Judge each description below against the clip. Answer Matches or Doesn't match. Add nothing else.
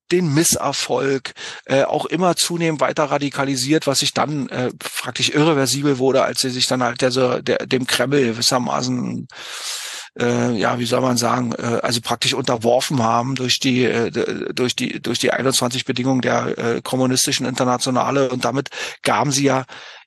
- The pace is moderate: Matches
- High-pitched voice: Doesn't match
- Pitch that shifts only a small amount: Matches